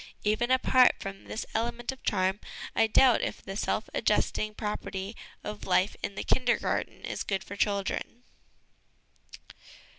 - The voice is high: Yes, high, 210 Hz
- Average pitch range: Yes, average, 3.4 semitones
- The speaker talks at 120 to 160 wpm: Yes, average, 140 wpm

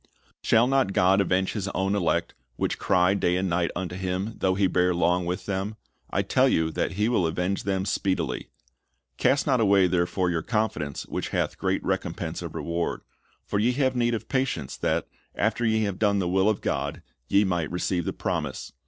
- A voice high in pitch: No, very low, 95 Hz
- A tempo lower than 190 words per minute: No, average, 195 wpm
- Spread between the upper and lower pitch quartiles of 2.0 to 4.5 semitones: Yes, average, 2.9 semitones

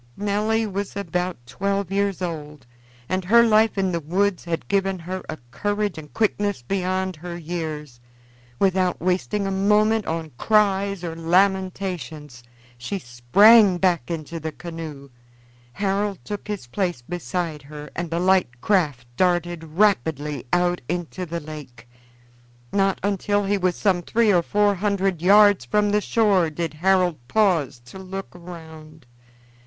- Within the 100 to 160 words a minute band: Yes, average, 145 wpm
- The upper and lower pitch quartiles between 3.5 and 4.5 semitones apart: Yes, average, 3.8 semitones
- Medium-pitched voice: Yes, medium, 180 Hz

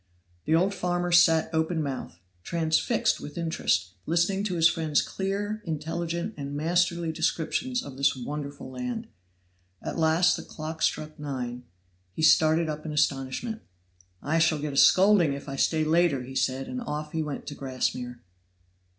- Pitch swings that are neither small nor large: Yes, average, 3.4 semitones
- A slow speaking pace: No, average, 160 wpm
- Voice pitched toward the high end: No, medium, 160 Hz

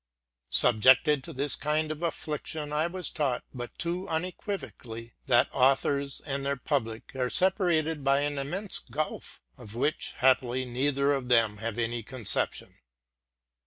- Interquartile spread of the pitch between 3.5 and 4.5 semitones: Yes, average, 3.9 semitones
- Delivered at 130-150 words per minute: Yes, average, 140 wpm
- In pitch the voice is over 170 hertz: No, medium, 140 Hz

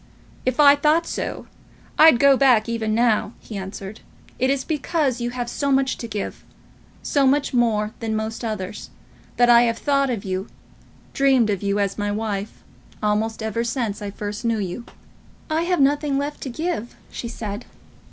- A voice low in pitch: No, high, 235 Hz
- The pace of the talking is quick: No, average, 175 wpm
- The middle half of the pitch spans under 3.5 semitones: No, average, 4.5 semitones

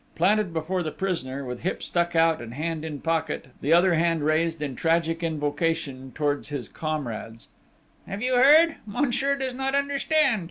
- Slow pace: No, average, 165 wpm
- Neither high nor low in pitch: Yes, medium, 165 Hz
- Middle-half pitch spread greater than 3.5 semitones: Yes, wide, 5.6 semitones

